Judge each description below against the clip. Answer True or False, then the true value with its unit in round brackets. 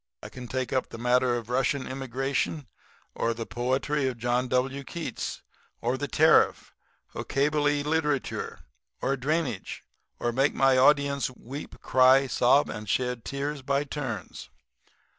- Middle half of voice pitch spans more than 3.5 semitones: False (2.4 semitones)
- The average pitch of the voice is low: True (130 Hz)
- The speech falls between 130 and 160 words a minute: True (140 wpm)